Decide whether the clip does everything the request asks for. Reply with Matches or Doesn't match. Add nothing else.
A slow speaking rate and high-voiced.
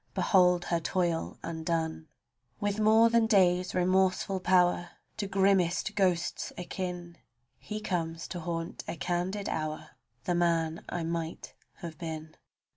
Doesn't match